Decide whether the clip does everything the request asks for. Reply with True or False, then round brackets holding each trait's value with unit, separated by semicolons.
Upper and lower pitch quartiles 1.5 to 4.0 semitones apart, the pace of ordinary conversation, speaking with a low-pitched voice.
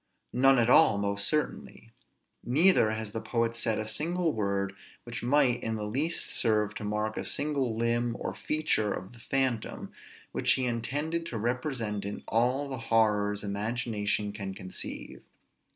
True (3.7 semitones; 155 wpm; 115 Hz)